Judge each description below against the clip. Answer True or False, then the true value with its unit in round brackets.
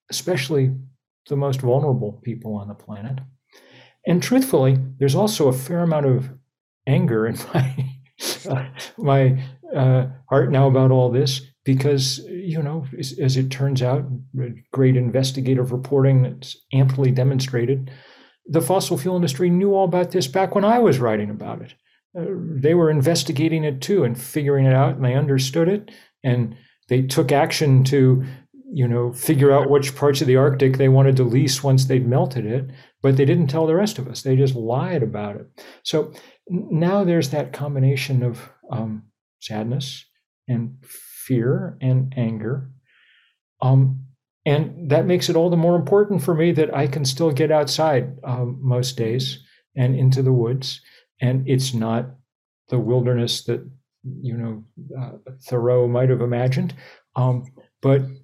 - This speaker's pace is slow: False (160 wpm)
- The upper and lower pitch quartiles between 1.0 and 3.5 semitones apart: True (2.9 semitones)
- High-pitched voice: False (135 Hz)